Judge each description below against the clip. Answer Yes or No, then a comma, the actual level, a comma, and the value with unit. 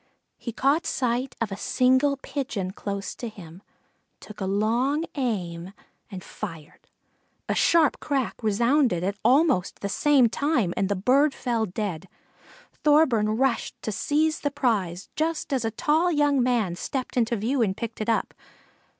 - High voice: Yes, high, 235 Hz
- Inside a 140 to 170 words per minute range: Yes, average, 155 wpm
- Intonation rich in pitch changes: Yes, wide, 5.7 semitones